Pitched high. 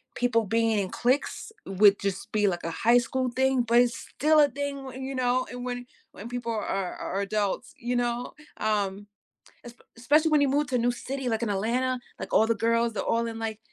Yes: high, 235 Hz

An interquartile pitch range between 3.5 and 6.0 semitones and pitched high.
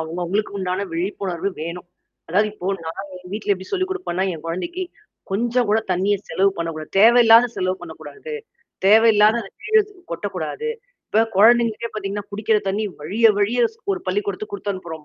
Yes: average, 4.2 semitones; high, 205 Hz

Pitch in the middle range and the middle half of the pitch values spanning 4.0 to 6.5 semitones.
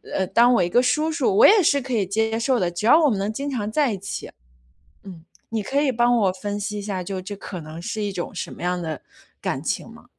No: high, 210 Hz; average, 4.9 semitones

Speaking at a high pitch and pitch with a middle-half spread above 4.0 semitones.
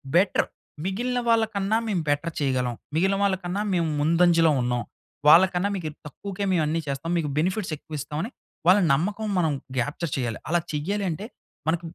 No: medium, 170 Hz; average, 4.5 semitones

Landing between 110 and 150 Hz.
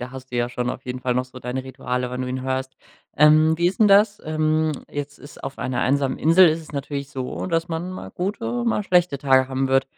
Yes: medium, 140 Hz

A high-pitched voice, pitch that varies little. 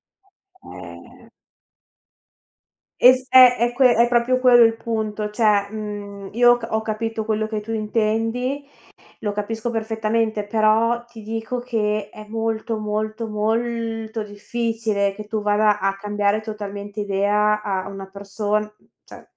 Yes: high, 220 Hz; narrow, 1.7 semitones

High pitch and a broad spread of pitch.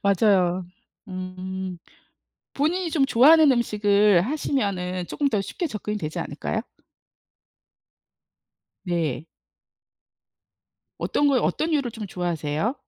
Yes: high, 205 Hz; wide, 7.0 semitones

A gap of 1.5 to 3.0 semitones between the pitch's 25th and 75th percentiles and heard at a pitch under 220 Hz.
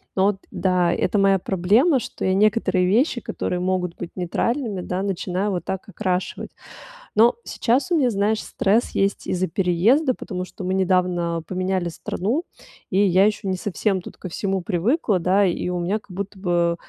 Yes: narrow, 2.6 semitones; high, 190 Hz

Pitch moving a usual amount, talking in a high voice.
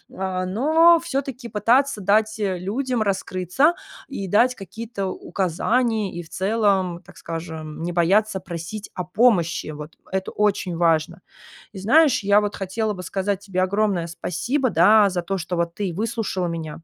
Yes: average, 3.9 semitones; high, 195 Hz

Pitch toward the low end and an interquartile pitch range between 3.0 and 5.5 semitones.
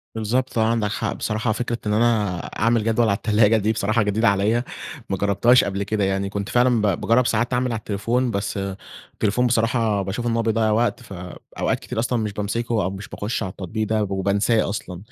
No: low, 110 Hz; narrow, 2.6 semitones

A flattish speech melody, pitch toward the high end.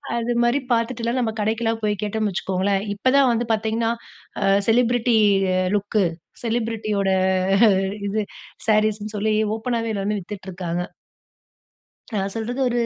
Yes: narrow, 2.3 semitones; high, 220 Hz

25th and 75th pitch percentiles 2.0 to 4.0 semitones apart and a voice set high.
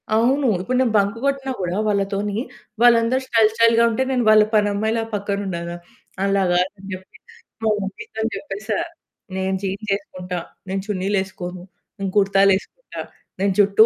Yes: average, 2.8 semitones; high, 200 Hz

